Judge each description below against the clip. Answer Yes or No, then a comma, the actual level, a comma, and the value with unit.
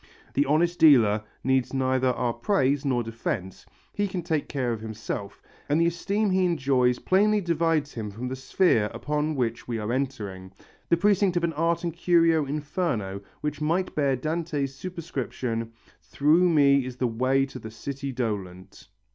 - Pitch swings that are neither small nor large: No, wide, 5.7 semitones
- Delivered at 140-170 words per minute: Yes, average, 165 wpm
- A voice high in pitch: No, medium, 140 Hz